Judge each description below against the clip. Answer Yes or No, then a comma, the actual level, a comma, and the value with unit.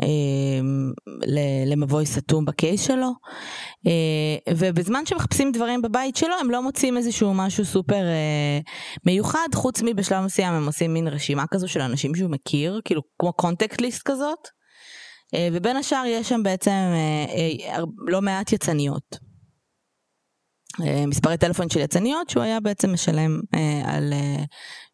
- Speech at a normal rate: Yes, average, 120 wpm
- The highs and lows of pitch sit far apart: Yes, wide, 7.4 semitones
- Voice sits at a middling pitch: Yes, medium, 175 Hz